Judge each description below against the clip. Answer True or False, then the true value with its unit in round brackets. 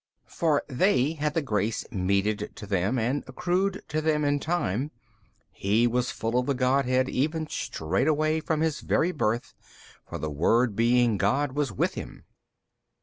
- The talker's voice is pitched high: False (130 Hz)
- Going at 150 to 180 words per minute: True (155 wpm)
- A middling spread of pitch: False (5.8 semitones)